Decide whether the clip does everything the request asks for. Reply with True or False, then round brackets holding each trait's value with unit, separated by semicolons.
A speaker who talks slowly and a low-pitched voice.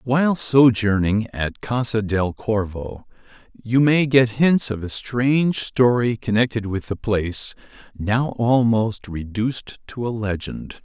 True (125 wpm; 115 Hz)